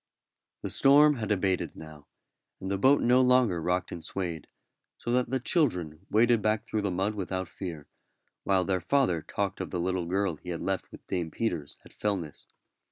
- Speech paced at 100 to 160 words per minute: No, average, 185 wpm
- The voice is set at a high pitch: No, very low, 95 Hz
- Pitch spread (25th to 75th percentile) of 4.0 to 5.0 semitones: Yes, average, 4.7 semitones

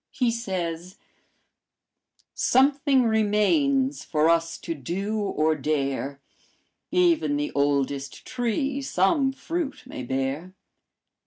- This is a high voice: Yes, high, 205 Hz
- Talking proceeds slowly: Yes, slow, 95 wpm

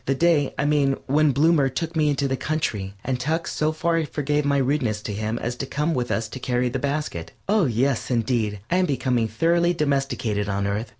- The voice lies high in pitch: No, low, 135 Hz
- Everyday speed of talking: No, fast, 215 wpm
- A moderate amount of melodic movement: Yes, average, 4.3 semitones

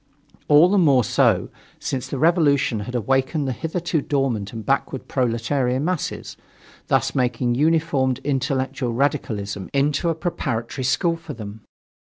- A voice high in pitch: No, low, 135 Hz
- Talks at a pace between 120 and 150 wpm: Yes, slow, 135 wpm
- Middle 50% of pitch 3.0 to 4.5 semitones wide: Yes, average, 3.9 semitones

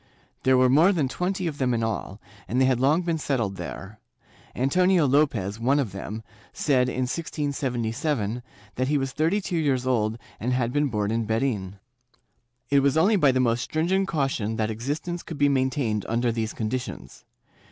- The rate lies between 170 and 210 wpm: Yes, average, 180 wpm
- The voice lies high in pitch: No, low, 130 Hz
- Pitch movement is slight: No, average, 4.6 semitones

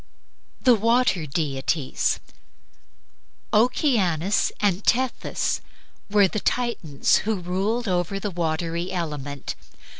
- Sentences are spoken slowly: Yes, slow, 90 wpm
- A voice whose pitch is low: No, medium, 185 Hz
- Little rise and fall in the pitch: No, average, 5.2 semitones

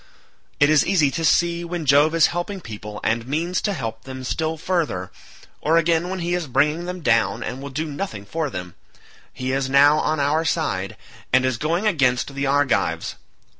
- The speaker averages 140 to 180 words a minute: No, average, 190 wpm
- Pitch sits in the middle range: Yes, medium, 150 Hz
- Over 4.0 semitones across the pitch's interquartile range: Yes, average, 4.5 semitones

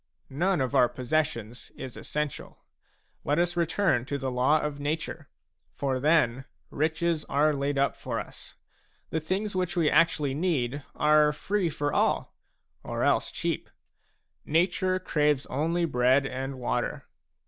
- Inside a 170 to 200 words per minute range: No, average, 140 wpm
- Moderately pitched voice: Yes, medium, 150 Hz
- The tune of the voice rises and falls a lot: No, average, 3.8 semitones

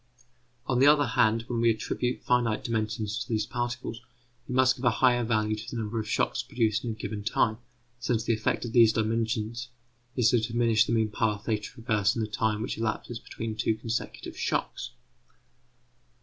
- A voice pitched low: Yes, low, 115 Hz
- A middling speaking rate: Yes, average, 190 wpm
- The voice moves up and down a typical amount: No, narrow, 1.8 semitones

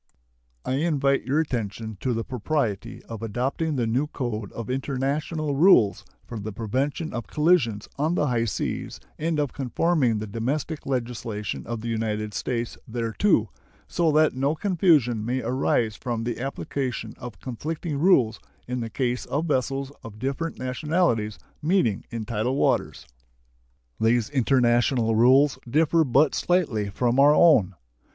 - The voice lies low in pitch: Yes, low, 125 Hz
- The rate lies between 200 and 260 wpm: No, average, 145 wpm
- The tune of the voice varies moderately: Yes, average, 4.6 semitones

